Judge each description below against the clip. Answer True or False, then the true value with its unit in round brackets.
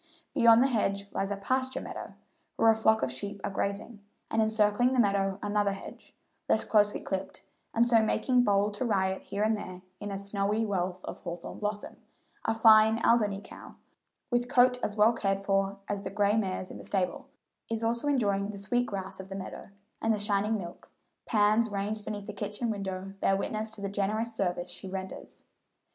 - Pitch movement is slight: True (2.2 semitones)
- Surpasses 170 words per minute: True (190 wpm)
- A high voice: True (205 Hz)